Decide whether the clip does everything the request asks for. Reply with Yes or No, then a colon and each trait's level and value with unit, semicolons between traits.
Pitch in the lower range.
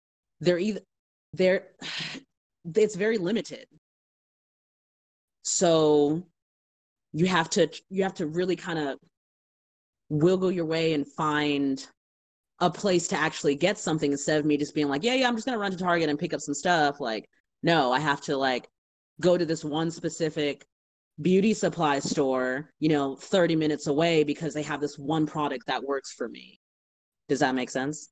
No: medium, 155 Hz